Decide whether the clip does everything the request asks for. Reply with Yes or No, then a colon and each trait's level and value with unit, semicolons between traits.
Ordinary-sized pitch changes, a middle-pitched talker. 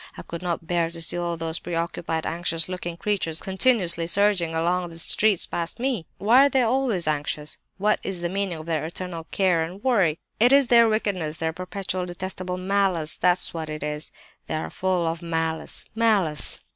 Yes: average, 3.3 semitones; medium, 175 Hz